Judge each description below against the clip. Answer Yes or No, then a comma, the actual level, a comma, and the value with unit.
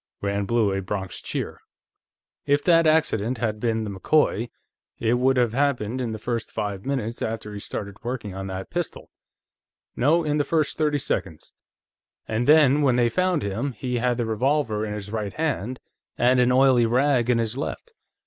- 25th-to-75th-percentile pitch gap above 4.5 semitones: Yes, average, 4.9 semitones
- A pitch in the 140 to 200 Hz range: No, low, 120 Hz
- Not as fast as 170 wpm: No, average, 180 wpm